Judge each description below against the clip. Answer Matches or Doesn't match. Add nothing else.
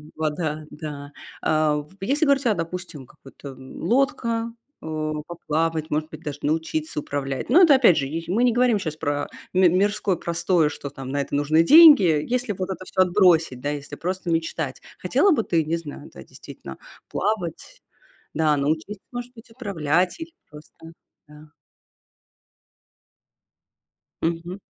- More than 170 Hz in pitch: Doesn't match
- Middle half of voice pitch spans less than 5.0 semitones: Doesn't match